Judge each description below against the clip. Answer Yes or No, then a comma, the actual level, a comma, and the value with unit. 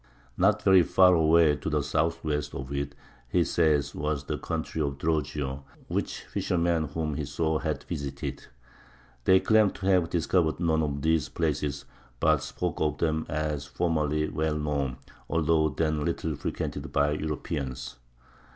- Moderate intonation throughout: No, narrow, 2.3 semitones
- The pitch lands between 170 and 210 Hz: No, very low, 75 Hz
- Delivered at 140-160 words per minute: Yes, average, 150 wpm